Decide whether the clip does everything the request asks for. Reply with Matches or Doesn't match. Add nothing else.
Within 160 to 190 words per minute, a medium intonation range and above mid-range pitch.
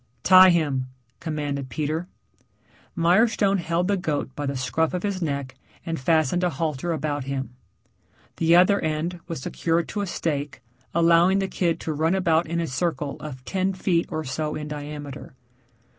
Doesn't match